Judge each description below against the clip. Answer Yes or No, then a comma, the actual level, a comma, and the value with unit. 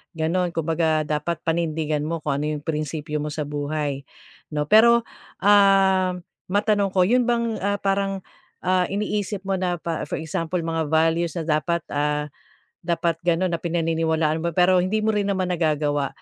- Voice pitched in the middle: Yes, medium, 170 Hz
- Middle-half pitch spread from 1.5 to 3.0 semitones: No, average, 3.7 semitones